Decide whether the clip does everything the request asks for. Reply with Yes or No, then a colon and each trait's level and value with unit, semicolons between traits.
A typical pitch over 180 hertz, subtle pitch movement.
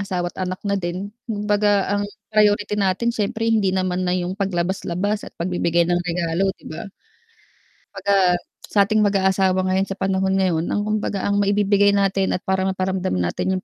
Yes: high, 190 Hz; narrow, 1.8 semitones